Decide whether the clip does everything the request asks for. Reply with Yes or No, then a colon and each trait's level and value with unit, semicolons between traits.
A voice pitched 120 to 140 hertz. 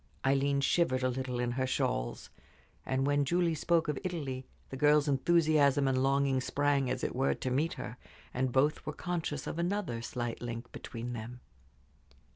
Yes: low, 135 Hz